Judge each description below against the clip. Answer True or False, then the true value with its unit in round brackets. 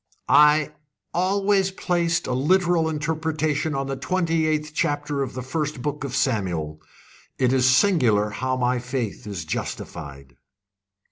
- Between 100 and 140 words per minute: True (135 wpm)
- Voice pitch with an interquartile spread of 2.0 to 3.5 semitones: False (4.4 semitones)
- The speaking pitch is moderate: True (145 Hz)